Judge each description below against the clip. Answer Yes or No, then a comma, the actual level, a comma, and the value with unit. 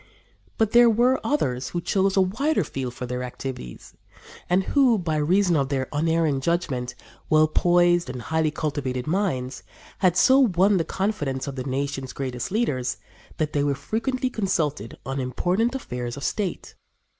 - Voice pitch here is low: No, medium, 155 Hz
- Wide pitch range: Yes, wide, 6.8 semitones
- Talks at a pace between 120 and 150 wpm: No, average, 160 wpm